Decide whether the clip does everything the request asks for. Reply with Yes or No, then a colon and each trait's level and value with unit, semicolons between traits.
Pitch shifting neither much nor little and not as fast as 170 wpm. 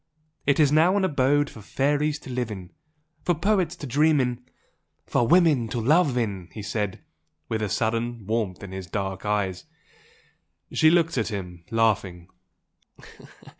No: wide, 6.5 semitones; average, 160 wpm